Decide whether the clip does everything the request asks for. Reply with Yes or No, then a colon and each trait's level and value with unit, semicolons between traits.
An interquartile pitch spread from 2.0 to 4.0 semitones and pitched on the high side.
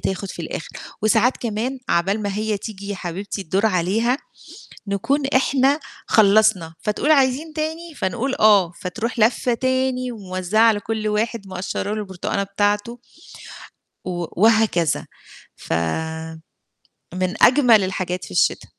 No: average, 4.5 semitones; high, 210 Hz